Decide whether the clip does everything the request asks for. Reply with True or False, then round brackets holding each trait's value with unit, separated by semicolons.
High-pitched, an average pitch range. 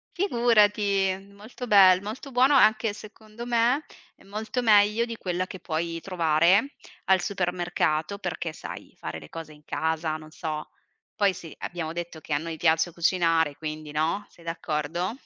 False (180 Hz; 4.7 semitones)